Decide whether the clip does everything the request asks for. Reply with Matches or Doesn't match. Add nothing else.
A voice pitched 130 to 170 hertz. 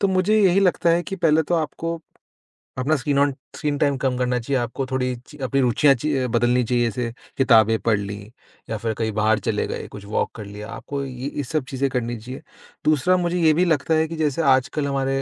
Matches